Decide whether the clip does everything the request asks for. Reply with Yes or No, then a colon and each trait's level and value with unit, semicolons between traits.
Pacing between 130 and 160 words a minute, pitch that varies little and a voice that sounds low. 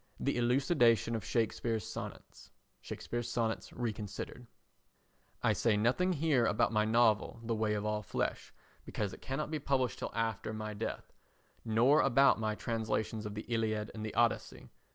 Yes: average, 155 wpm; narrow, 2.1 semitones; low, 115 Hz